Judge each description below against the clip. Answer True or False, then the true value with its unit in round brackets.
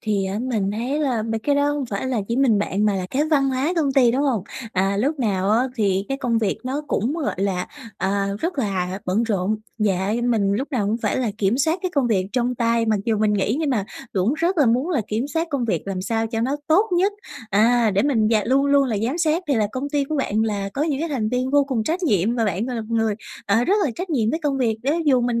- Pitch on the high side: True (235 Hz)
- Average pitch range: True (5.0 semitones)